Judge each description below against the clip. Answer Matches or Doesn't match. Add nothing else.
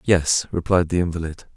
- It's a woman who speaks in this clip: Doesn't match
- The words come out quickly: Doesn't match